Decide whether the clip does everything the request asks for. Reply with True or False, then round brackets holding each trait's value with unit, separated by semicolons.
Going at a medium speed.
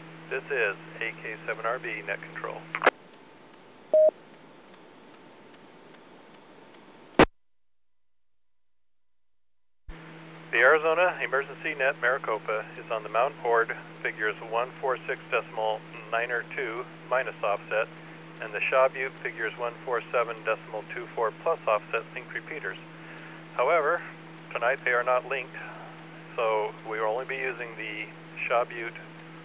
False (100 wpm)